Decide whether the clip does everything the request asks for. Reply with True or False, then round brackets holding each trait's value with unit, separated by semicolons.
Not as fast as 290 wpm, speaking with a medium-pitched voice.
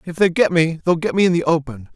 False (305 wpm; 165 Hz)